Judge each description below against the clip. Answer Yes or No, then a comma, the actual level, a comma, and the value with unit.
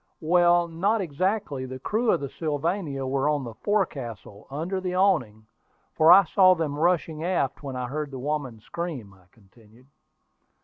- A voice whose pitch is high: No, medium, 150 Hz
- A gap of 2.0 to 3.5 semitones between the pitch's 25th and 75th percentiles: No, wide, 5.5 semitones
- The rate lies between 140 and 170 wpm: Yes, average, 165 wpm